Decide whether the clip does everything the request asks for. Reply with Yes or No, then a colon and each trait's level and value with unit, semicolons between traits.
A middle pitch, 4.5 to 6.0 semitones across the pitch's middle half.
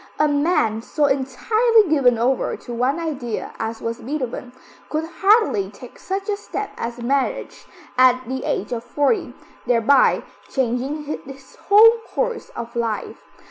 No: very high, 270 Hz; wide, 5.6 semitones